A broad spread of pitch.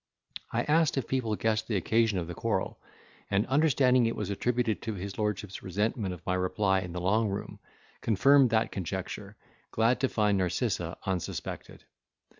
No: average, 3.7 semitones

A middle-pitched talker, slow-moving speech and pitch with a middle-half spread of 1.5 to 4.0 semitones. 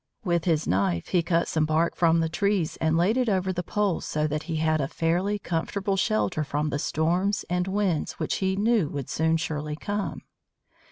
No: medium, 170 Hz; average, 200 wpm; average, 3.6 semitones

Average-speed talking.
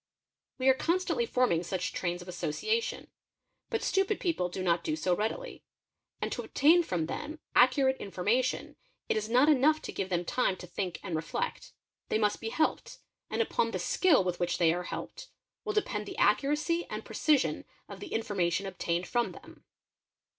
Yes: average, 185 wpm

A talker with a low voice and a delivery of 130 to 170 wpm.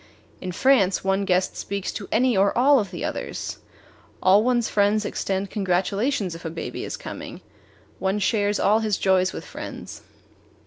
No: high, 200 Hz; average, 165 wpm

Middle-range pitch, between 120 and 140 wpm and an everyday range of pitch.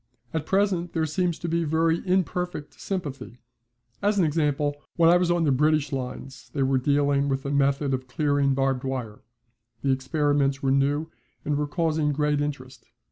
No: medium, 145 Hz; average, 175 wpm; average, 3.1 semitones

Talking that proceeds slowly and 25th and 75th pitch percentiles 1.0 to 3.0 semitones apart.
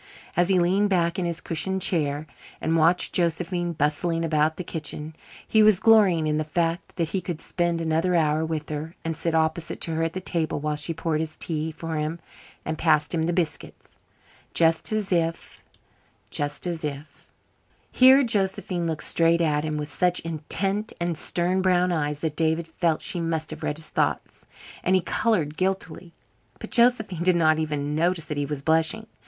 No: average, 185 wpm; narrow, 2.4 semitones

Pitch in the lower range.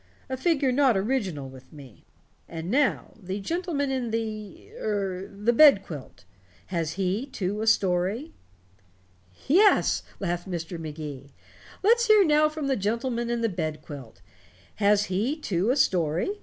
No: high, 205 Hz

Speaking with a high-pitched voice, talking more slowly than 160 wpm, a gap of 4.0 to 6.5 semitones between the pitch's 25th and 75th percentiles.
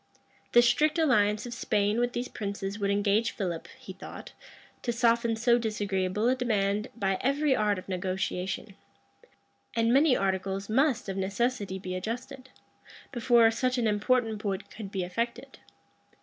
No: high, 220 Hz; average, 150 wpm; average, 3.6 semitones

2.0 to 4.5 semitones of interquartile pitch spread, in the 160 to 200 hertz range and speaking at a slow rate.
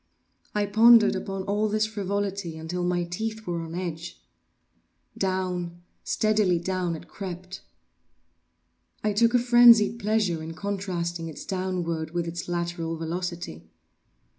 Yes: average, 3.3 semitones; medium, 185 Hz; slow, 120 wpm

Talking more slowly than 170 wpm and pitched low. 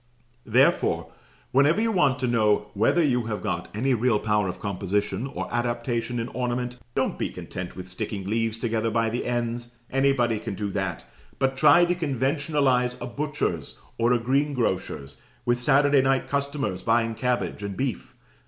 Yes: average, 160 wpm; low, 120 Hz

